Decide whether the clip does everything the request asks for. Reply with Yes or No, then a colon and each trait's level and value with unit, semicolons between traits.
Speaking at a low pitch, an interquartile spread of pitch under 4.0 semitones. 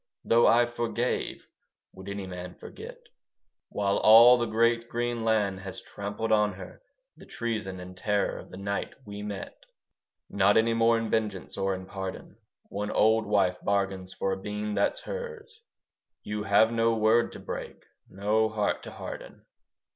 Yes: low, 105 Hz; average, 2.7 semitones